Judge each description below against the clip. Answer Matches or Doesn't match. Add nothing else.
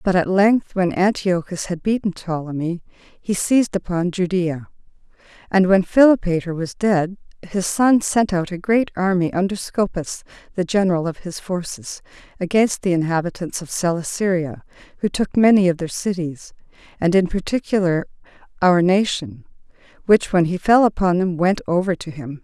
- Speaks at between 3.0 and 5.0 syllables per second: Matches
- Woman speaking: Matches